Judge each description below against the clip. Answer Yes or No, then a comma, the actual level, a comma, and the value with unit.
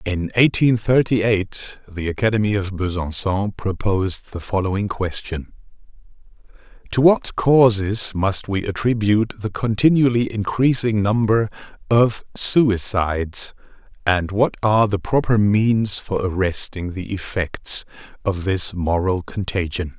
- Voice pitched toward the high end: No, low, 100 Hz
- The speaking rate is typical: No, slow, 115 wpm